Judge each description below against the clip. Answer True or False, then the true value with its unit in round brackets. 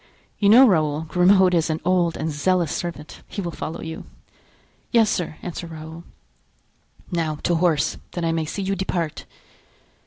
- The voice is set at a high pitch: False (170 Hz)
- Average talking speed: True (160 wpm)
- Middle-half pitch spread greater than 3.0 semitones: False (2.5 semitones)